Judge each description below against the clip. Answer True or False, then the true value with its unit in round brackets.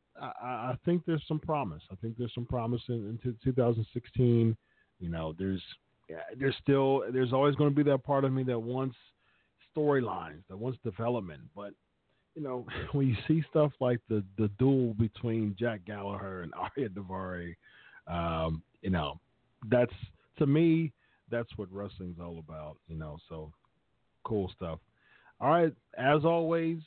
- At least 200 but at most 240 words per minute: False (160 wpm)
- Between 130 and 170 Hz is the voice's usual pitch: False (120 Hz)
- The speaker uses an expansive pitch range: True (6.0 semitones)